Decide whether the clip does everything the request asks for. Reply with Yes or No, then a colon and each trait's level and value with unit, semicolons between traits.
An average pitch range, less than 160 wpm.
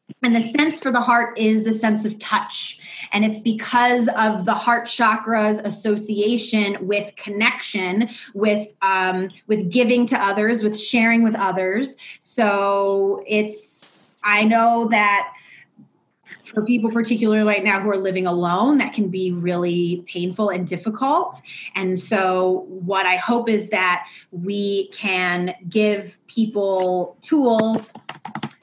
Yes: average, 3.0 semitones; slow, 135 wpm